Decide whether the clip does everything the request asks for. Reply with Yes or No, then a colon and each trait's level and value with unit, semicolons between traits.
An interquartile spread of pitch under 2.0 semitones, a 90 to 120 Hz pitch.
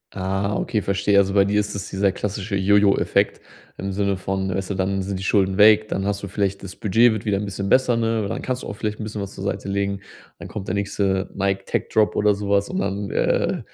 Yes: narrow, 1.2 semitones; low, 100 Hz